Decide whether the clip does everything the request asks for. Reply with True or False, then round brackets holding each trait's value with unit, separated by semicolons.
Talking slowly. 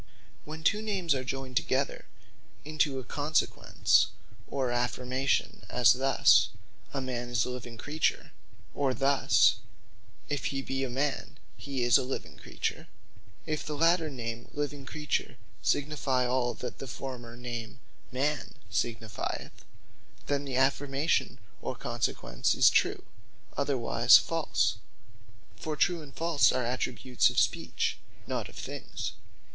True (130 wpm)